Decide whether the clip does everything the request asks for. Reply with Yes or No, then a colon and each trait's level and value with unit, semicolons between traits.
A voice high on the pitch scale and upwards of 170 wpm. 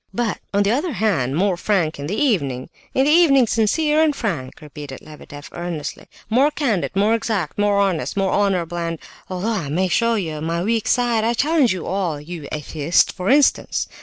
Yes: high, 195 Hz; average, 190 wpm